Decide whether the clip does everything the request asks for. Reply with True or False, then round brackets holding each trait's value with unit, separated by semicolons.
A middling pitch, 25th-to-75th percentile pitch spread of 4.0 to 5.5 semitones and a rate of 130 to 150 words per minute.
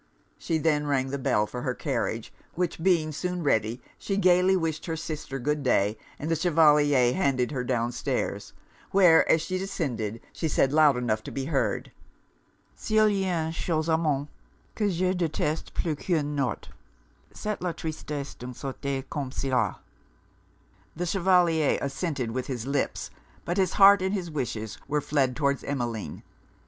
False (150 Hz; 4.7 semitones; 160 wpm)